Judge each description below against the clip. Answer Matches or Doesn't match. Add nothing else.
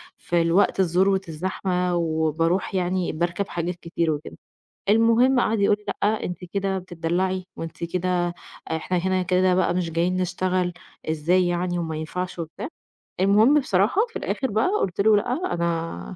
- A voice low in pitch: Doesn't match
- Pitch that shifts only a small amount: Matches